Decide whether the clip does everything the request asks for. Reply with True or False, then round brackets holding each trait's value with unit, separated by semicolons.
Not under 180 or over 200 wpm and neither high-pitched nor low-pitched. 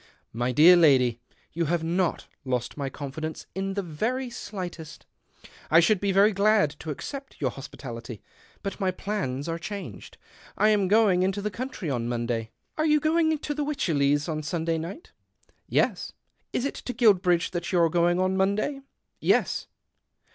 True (190 wpm; 180 Hz)